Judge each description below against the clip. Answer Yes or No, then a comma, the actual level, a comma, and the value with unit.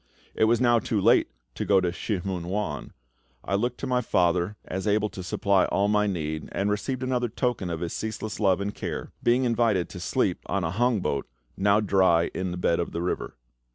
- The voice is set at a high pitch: No, low, 100 Hz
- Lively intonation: No, average, 3.8 semitones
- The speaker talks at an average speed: No, fast, 220 wpm